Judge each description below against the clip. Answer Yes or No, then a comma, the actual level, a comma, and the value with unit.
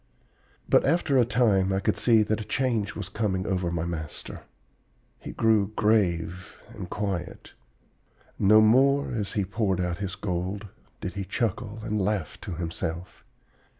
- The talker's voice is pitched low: Yes, low, 100 Hz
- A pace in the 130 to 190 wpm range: Yes, average, 150 wpm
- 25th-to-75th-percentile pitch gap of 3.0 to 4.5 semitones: Yes, average, 3.3 semitones